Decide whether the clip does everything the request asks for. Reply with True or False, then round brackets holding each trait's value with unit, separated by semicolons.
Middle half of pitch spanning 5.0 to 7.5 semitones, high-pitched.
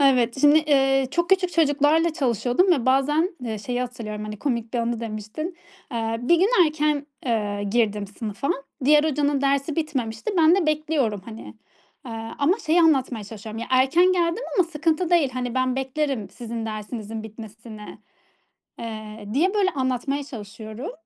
True (5.5 semitones; 260 Hz)